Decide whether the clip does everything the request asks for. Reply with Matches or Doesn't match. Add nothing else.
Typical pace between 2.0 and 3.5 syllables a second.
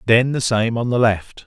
Doesn't match